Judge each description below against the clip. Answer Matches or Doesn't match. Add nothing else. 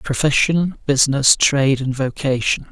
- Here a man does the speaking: Matches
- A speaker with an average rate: Doesn't match